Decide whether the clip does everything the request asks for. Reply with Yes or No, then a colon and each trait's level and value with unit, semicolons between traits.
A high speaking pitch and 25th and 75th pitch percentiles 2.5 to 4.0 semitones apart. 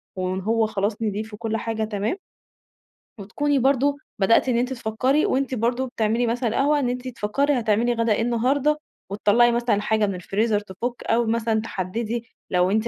Yes: high, 230 Hz; average, 2.8 semitones